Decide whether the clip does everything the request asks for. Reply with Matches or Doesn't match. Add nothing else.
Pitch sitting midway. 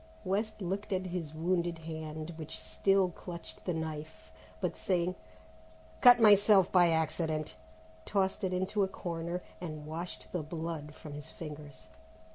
Matches